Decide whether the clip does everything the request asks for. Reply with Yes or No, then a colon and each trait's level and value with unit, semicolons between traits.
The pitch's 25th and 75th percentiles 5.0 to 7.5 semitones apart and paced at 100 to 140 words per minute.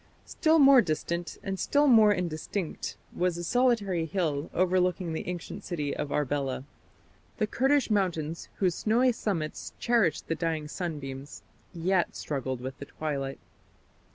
Yes: wide, 5.4 semitones; slow, 135 wpm